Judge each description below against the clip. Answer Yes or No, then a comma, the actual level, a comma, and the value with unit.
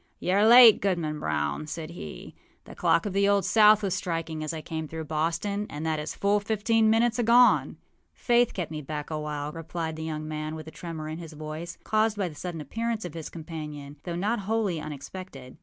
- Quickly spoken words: Yes, fast, 210 wpm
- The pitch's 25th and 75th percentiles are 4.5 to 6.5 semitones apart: Yes, average, 4.9 semitones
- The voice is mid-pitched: Yes, medium, 165 Hz